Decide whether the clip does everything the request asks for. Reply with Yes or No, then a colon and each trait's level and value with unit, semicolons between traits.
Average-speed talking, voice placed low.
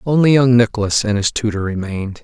Yes: average, 190 wpm; low, 115 Hz